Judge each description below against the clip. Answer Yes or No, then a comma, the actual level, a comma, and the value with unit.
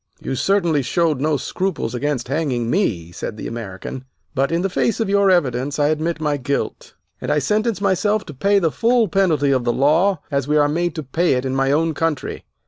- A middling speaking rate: No, fast, 215 wpm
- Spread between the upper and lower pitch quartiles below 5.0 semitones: No, wide, 5.4 semitones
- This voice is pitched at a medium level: Yes, medium, 150 Hz